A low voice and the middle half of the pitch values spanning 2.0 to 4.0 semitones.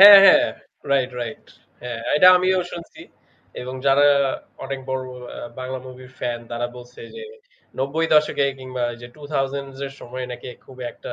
Yes: low, 130 Hz; average, 3.1 semitones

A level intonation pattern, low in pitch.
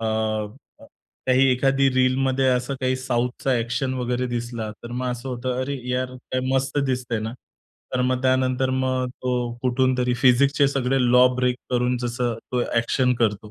Yes: narrow, 1.2 semitones; low, 125 Hz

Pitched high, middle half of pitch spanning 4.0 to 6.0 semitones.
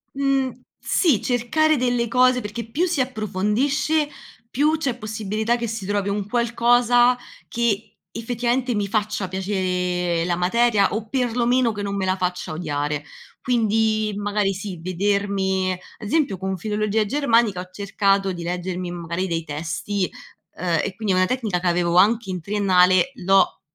Yes: high, 205 Hz; average, 4.4 semitones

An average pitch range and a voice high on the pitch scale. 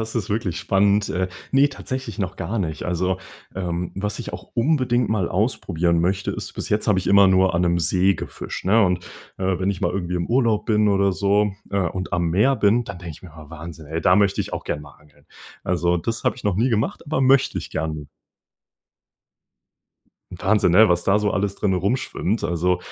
No: average, 3.2 semitones; very low, 95 Hz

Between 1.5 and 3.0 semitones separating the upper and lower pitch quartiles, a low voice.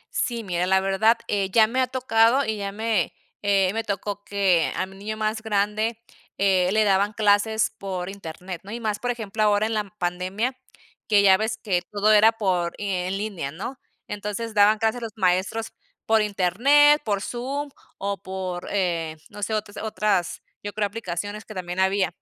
No: narrow, 2.5 semitones; high, 205 Hz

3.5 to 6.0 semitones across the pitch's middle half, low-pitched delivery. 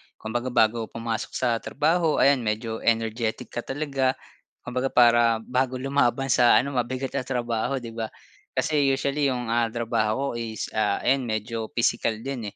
No: average, 2.9 semitones; low, 120 Hz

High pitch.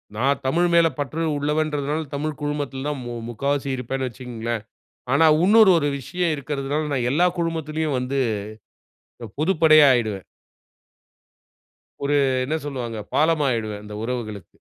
No: medium, 140 Hz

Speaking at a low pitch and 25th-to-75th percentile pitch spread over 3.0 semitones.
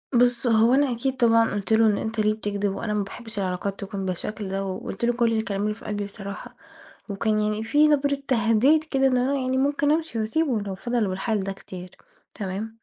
No: high, 220 Hz; average, 3.7 semitones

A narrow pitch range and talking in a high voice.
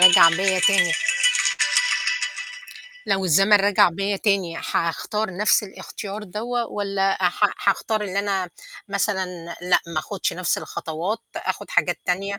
Yes: narrow, 2.2 semitones; high, 195 Hz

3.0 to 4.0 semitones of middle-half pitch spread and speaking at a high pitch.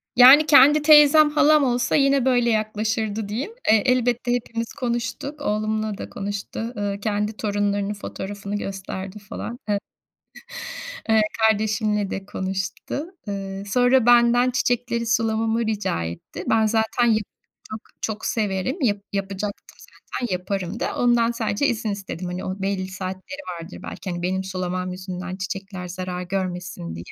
Yes: average, 3.7 semitones; high, 210 Hz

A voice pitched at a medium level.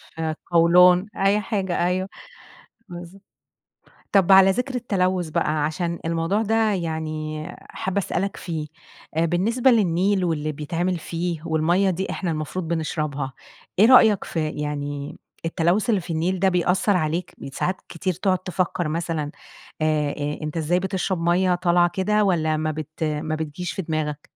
Yes: medium, 175 Hz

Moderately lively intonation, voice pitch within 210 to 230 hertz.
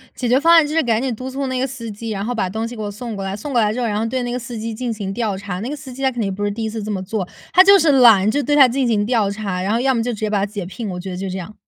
Yes: average, 3.7 semitones; high, 225 Hz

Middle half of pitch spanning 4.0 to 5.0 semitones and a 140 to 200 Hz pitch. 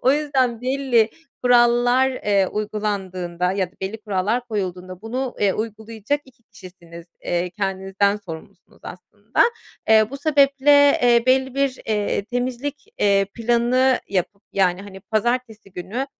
No: average, 4.7 semitones; high, 220 Hz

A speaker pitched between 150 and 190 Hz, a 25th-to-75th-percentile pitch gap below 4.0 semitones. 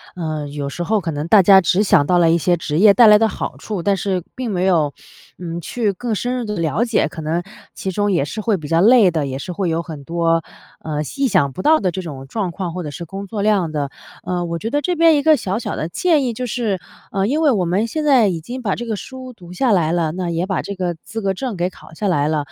No: medium, 185 Hz; average, 4.9 semitones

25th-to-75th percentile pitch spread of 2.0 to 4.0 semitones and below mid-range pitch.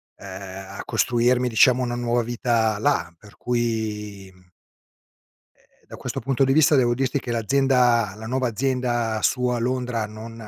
Yes: narrow, 2.6 semitones; low, 120 Hz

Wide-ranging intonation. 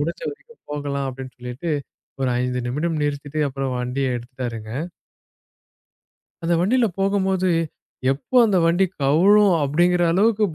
Yes: wide, 6.2 semitones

